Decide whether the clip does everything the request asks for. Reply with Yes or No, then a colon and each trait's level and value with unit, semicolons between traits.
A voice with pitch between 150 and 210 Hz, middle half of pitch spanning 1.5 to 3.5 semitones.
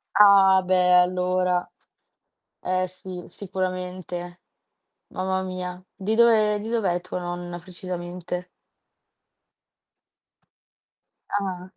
No: medium, 185 Hz; narrow, 1.0 semitones